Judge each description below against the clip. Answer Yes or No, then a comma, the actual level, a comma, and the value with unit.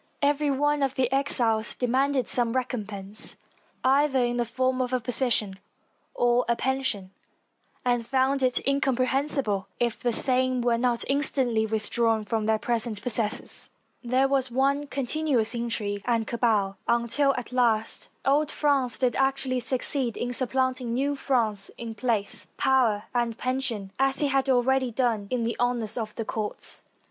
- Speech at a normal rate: Yes, average, 150 wpm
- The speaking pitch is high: Yes, high, 245 Hz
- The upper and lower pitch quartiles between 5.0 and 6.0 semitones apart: No, average, 2.7 semitones